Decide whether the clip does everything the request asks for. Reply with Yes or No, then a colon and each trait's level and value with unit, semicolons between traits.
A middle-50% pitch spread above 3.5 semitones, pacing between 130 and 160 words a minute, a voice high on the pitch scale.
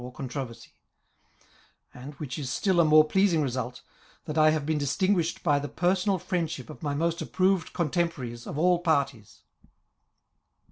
No: average, 4.1 semitones; average, 155 wpm; medium, 155 Hz